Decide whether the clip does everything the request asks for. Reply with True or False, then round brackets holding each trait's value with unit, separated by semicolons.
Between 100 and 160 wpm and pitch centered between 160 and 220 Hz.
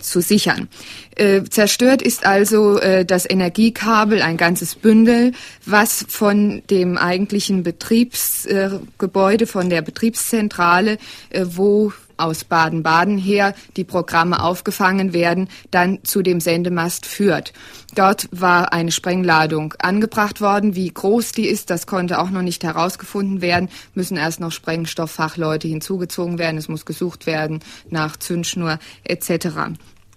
True (130 wpm; 185 Hz)